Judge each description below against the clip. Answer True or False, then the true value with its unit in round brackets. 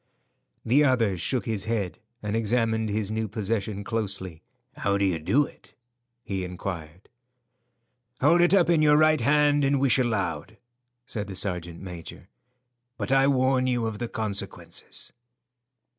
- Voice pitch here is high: False (110 Hz)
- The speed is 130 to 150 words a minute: True (145 wpm)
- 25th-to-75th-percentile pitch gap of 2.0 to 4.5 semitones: False (5.2 semitones)